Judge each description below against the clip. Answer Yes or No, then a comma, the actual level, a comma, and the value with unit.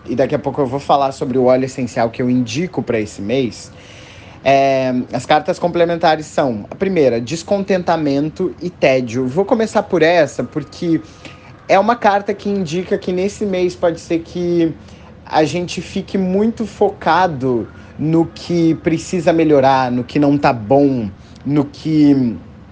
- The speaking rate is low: No, average, 155 wpm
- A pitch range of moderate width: No, wide, 5.8 semitones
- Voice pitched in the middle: Yes, medium, 155 Hz